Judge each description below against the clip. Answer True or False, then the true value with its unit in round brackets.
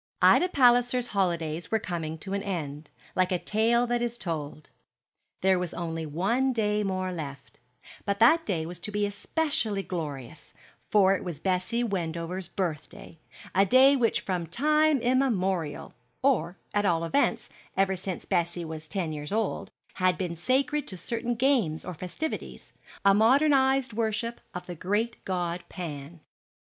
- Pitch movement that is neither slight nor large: False (5.7 semitones)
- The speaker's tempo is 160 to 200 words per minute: False (150 wpm)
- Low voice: False (190 Hz)